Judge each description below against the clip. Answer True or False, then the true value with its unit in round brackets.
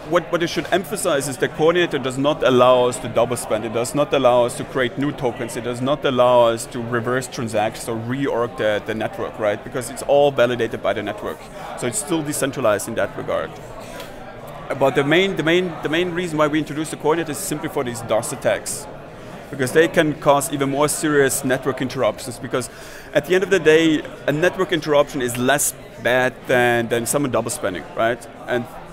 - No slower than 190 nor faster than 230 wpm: True (205 wpm)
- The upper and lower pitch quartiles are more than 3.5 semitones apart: True (3.9 semitones)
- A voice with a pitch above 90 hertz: True (140 Hz)